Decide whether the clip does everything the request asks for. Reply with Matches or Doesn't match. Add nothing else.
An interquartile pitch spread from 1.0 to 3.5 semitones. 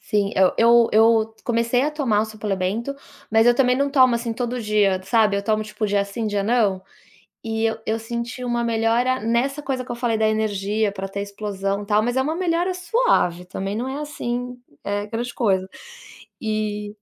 Matches